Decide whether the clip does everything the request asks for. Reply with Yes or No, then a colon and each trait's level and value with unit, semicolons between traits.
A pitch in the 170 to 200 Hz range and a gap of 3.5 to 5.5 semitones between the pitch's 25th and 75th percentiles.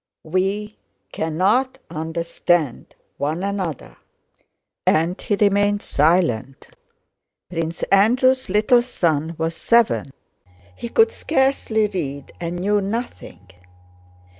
Yes: medium, 185 Hz; average, 4.8 semitones